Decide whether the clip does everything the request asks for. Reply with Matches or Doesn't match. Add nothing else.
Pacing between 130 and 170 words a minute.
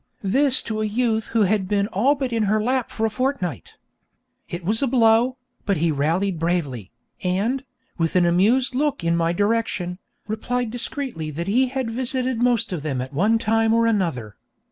Doesn't match